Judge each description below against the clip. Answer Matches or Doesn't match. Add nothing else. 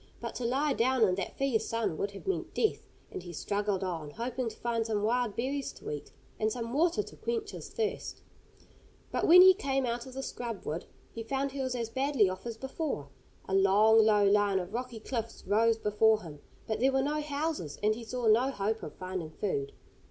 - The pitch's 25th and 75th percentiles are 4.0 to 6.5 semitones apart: Matches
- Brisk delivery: Matches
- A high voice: Matches